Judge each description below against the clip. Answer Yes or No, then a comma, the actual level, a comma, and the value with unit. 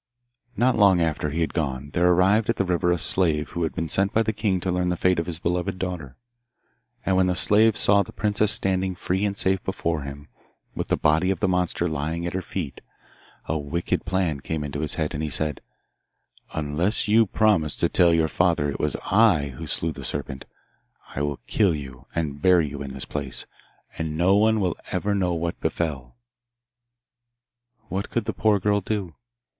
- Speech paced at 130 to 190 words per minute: No, average, 200 wpm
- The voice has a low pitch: Yes, very low, 85 Hz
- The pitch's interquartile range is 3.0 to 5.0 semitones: Yes, average, 4.0 semitones